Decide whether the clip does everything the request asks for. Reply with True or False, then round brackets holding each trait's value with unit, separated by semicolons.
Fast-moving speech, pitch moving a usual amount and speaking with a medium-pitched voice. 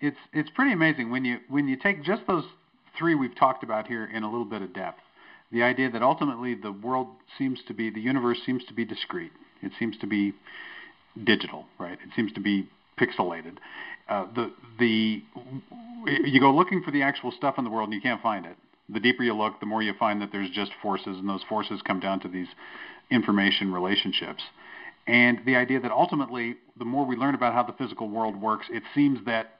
False (215 wpm; 3.7 semitones; 120 Hz)